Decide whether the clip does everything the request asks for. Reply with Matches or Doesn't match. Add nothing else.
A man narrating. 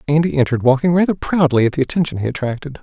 Matches